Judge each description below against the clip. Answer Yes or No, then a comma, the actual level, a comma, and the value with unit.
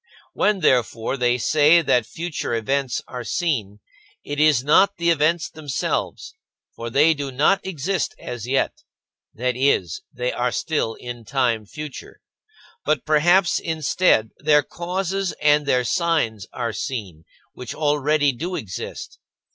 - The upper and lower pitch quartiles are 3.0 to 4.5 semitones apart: No, average, 5.1 semitones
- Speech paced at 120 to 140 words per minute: Yes, slow, 135 wpm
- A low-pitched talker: No, medium, 145 Hz